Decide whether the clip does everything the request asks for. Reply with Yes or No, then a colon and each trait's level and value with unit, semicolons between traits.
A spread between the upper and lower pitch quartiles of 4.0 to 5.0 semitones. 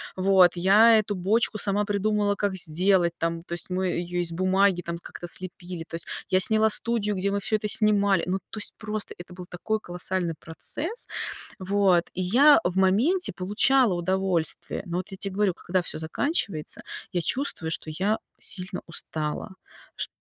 No: average, 2.9 semitones